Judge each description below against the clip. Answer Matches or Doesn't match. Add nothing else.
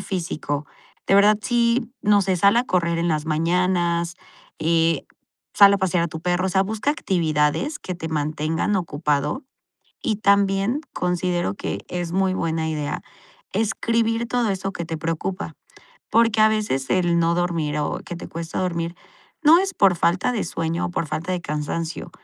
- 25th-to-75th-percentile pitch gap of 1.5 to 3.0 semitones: Doesn't match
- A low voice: Doesn't match